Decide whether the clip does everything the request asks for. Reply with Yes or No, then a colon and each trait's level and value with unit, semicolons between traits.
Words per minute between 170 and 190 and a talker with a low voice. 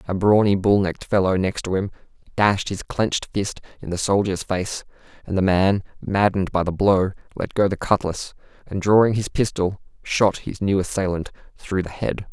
Yes: average, 180 wpm; very low, 95 Hz